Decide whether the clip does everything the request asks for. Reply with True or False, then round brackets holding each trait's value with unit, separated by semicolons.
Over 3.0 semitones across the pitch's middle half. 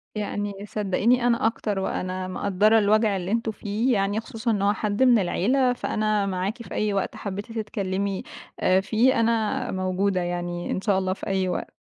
False (2.7 semitones)